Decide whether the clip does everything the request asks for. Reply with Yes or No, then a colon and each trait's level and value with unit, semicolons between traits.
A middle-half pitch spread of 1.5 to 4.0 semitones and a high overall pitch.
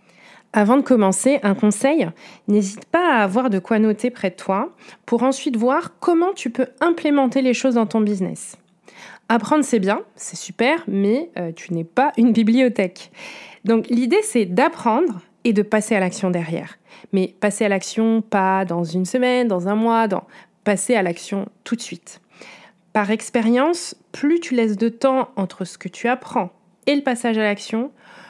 No: average, 4.8 semitones; high, 225 Hz